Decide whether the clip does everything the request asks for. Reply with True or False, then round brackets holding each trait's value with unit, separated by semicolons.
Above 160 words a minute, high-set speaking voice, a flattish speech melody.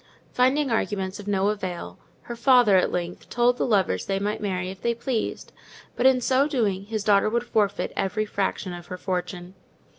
False (185 wpm; 205 Hz; 4.0 semitones)